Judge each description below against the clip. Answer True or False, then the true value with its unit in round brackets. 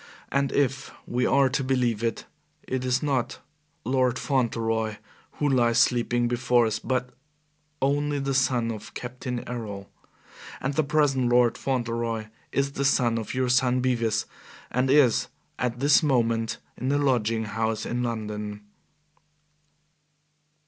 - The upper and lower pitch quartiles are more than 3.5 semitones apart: False (2.6 semitones)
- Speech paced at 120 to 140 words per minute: True (135 wpm)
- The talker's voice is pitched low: True (125 Hz)